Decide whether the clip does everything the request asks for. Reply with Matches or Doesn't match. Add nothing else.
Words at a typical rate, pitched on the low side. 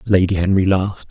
Matches